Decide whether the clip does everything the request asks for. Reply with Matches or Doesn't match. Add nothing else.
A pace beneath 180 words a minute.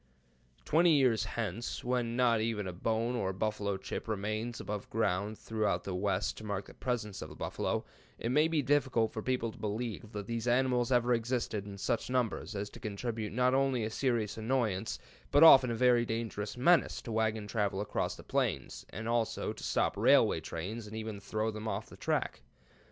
Doesn't match